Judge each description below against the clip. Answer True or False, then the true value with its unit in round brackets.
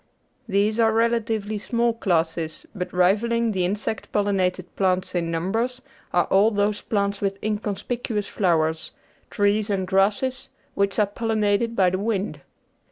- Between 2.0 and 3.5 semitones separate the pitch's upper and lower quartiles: True (3.0 semitones)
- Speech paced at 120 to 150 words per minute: True (140 wpm)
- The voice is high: True (205 Hz)